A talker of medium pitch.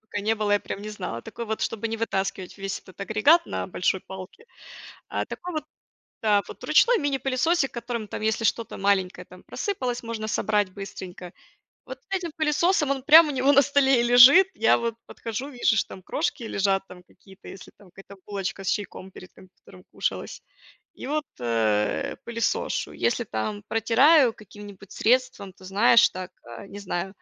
No: high, 220 Hz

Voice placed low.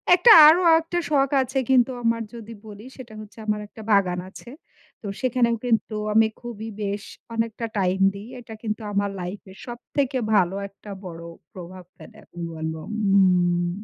No: high, 215 Hz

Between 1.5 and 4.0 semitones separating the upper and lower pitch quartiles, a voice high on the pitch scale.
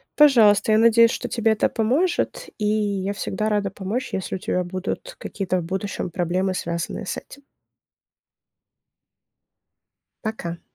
Yes: average, 3.2 semitones; high, 205 Hz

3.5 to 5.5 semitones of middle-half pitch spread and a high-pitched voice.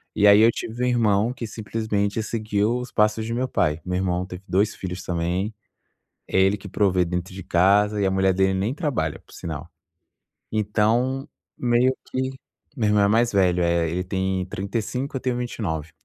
No: average, 3.8 semitones; low, 105 Hz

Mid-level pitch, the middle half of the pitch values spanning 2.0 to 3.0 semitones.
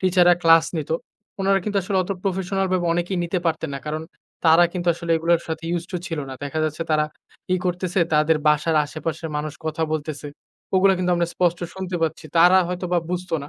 Yes: medium, 170 Hz; narrow, 2.4 semitones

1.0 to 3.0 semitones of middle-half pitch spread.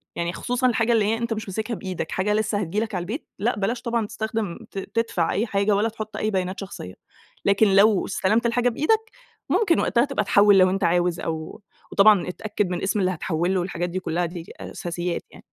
No: average, 3.8 semitones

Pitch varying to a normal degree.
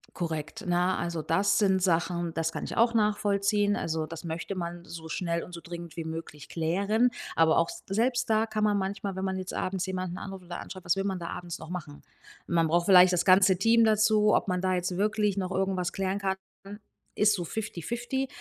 Yes: average, 3.1 semitones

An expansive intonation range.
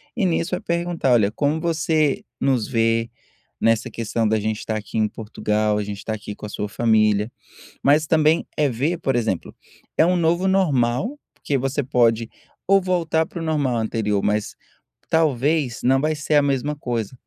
Yes: wide, 6.3 semitones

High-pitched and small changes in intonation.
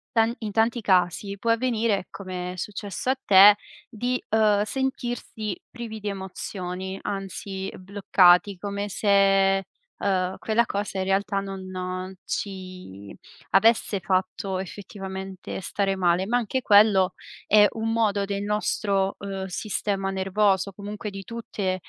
Yes: high, 195 Hz; narrow, 1.9 semitones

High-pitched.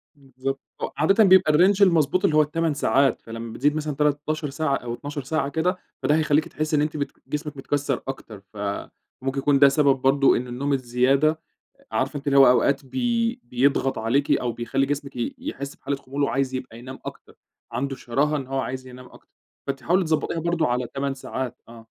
No: medium, 140 Hz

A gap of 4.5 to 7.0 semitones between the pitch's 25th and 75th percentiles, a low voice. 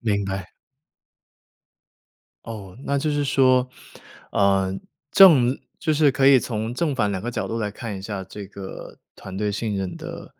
Yes: average, 4.9 semitones; low, 110 Hz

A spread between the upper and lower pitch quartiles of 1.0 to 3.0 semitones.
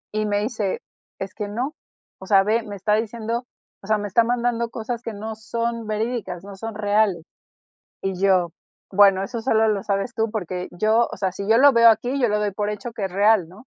Yes: narrow, 2.6 semitones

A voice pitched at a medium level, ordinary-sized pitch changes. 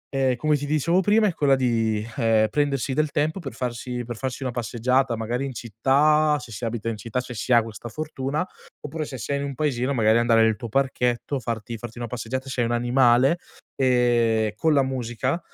No: low, 125 Hz; average, 3.1 semitones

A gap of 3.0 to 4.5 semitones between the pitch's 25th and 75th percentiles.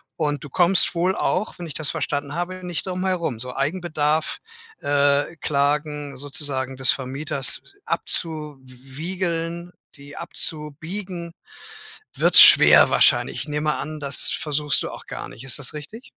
Yes: average, 3.3 semitones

